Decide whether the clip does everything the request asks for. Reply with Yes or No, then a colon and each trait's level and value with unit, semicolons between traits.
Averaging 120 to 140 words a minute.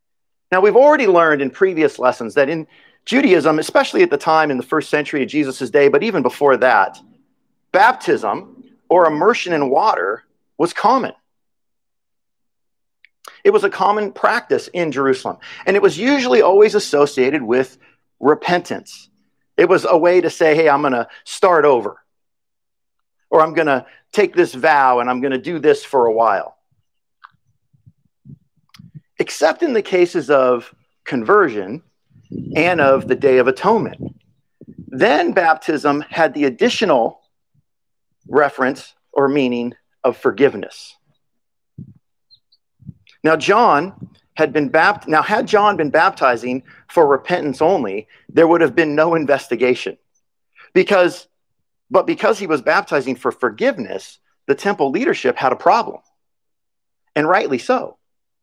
Yes: slow, 135 wpm